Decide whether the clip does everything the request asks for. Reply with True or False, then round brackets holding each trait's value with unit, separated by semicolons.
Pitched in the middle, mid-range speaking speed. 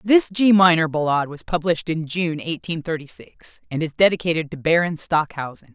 True (165 Hz; 180 wpm)